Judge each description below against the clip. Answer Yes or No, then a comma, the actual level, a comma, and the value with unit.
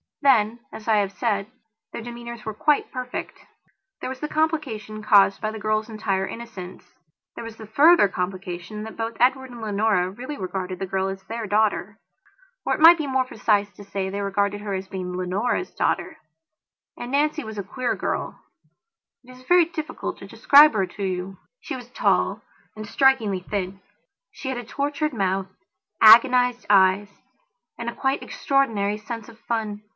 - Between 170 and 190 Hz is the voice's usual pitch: No, high, 220 Hz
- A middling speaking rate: Yes, average, 175 wpm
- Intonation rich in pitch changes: No, average, 4.2 semitones